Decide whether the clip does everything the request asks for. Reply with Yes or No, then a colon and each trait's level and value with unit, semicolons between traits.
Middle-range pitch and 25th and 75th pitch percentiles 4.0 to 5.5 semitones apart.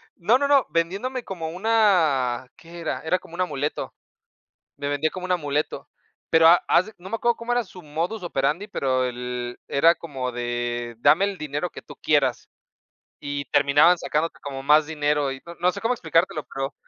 Yes: medium, 160 Hz; average, 4.7 semitones